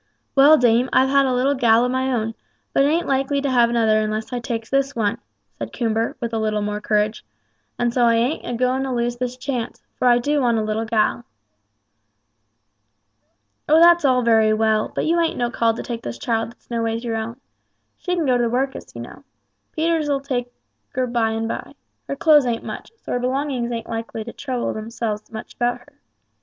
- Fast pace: Yes, fast, 210 wpm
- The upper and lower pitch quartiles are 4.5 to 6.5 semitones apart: No, average, 3.0 semitones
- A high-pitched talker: Yes, high, 240 Hz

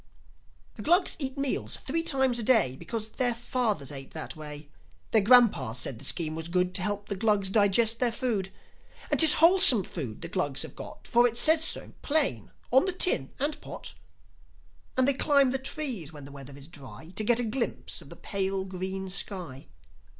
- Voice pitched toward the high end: Yes, high, 210 Hz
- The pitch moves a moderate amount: No, wide, 7.9 semitones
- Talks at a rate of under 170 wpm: No, average, 195 wpm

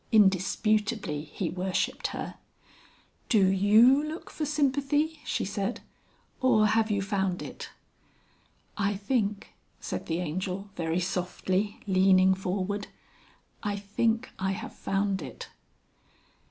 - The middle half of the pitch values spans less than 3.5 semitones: Yes, average, 2.9 semitones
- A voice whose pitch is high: Yes, high, 200 Hz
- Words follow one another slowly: Yes, slow, 115 wpm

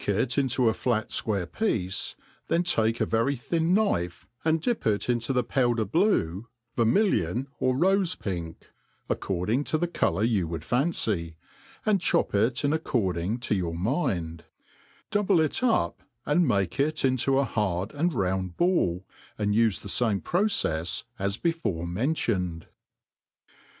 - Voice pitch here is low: Yes, low, 115 Hz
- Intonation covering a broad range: Yes, wide, 8.7 semitones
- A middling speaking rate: Yes, average, 150 wpm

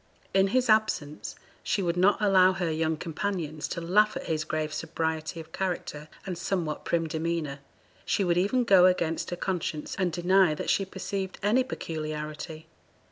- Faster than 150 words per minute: Yes, average, 165 wpm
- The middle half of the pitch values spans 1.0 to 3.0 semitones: No, average, 3.4 semitones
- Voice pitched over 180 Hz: No, medium, 175 Hz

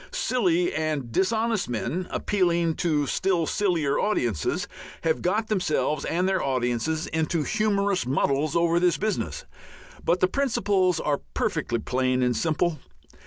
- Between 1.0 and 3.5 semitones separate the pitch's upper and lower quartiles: No, average, 4.7 semitones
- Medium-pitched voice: Yes, medium, 170 Hz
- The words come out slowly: Yes, slow, 130 wpm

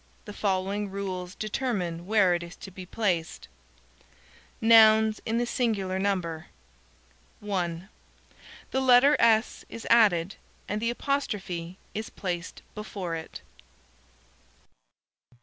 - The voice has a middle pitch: No, high, 200 Hz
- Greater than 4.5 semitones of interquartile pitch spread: No, average, 3.7 semitones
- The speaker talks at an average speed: No, slow, 115 wpm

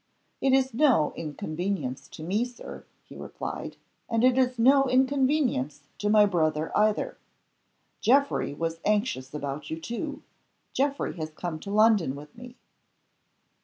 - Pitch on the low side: No, high, 210 Hz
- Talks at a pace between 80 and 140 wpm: Yes, slow, 135 wpm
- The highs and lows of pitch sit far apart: Yes, wide, 8.6 semitones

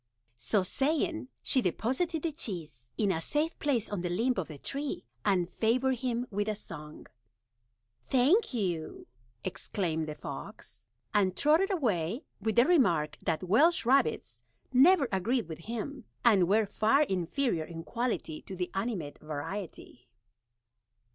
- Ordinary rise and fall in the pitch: No, wide, 7.4 semitones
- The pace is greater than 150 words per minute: No, average, 140 wpm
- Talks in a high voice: Yes, high, 215 Hz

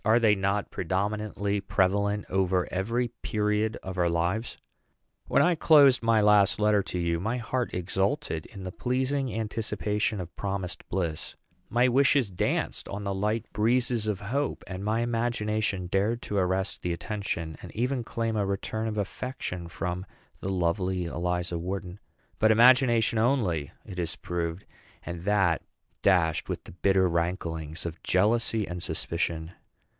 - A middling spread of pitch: Yes, average, 4.0 semitones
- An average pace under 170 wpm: Yes, average, 150 wpm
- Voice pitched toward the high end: No, low, 100 Hz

